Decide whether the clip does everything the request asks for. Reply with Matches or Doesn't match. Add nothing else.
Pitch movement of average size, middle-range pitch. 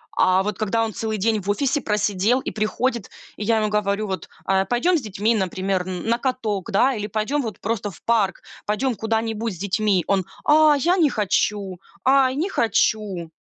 Doesn't match